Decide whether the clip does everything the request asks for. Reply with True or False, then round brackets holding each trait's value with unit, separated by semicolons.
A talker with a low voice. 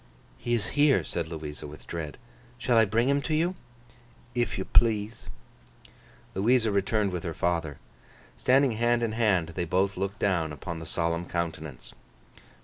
True (100 Hz)